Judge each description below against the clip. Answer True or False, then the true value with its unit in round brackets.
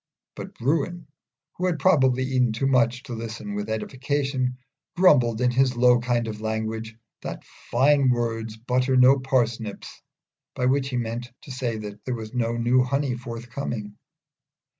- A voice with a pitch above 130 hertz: False (125 Hz)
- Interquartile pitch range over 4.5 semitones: False (2.5 semitones)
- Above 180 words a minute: False (155 wpm)